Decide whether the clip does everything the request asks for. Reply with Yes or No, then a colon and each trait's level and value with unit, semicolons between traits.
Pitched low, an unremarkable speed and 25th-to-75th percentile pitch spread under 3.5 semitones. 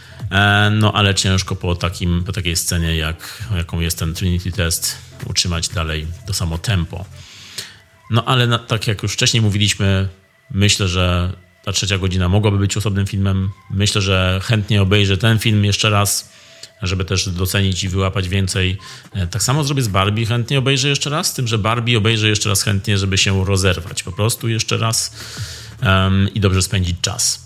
No: low, 100 Hz; fast, 175 wpm; average, 2.9 semitones